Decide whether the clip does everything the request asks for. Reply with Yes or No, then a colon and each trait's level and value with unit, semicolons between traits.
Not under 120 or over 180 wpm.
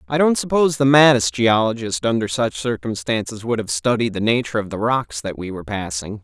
No: average, 200 wpm